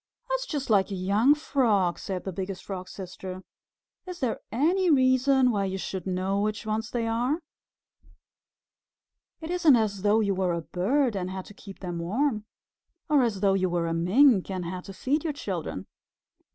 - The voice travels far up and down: Yes, wide, 5.7 semitones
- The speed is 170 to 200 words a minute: Yes, average, 180 wpm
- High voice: Yes, high, 205 Hz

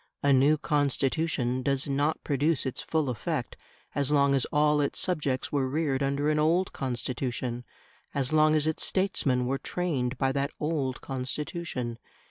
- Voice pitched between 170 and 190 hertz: No, medium, 140 Hz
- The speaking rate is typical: Yes, average, 155 wpm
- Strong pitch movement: No, average, 2.7 semitones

